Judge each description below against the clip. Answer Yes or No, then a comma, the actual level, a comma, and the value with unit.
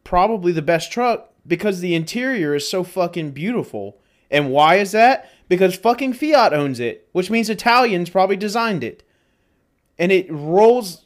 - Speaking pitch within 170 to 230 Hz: Yes, medium, 185 Hz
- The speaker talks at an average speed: Yes, average, 155 wpm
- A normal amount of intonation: No, wide, 5.8 semitones